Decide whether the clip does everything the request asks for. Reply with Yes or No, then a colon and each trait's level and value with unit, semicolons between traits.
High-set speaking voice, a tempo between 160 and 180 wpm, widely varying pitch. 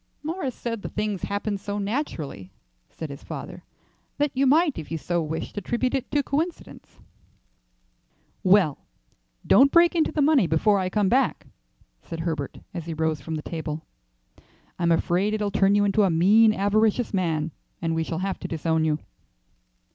Yes: high, 195 Hz; average, 170 wpm; wide, 6.6 semitones